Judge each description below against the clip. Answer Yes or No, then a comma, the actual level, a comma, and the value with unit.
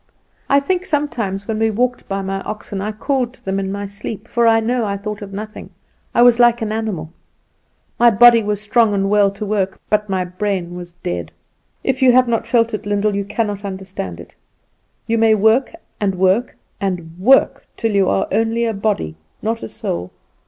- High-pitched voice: Yes, high, 210 Hz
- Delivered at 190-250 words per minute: Yes, average, 200 wpm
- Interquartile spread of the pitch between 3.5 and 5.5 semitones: No, average, 2.9 semitones